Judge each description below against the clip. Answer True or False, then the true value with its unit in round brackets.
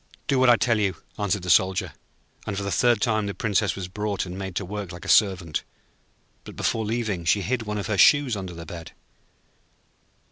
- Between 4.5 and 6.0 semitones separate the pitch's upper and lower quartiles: False (2.8 semitones)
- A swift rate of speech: True (210 wpm)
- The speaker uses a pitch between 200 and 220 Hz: False (100 Hz)